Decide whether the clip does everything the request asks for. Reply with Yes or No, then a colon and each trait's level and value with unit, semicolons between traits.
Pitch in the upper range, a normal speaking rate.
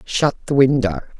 No: low, 125 Hz; average, 150 wpm